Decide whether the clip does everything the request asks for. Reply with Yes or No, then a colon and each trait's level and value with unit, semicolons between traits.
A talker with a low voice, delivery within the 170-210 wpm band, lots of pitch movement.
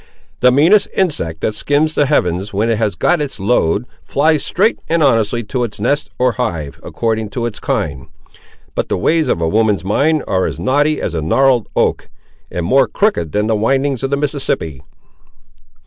Yes: low, 120 Hz; average, 185 wpm; wide, 5.9 semitones